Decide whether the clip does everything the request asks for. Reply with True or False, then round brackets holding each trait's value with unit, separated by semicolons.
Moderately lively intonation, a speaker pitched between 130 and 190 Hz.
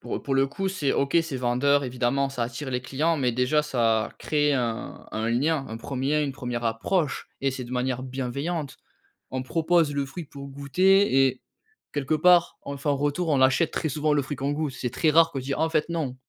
True (3.1 semitones; 140 Hz)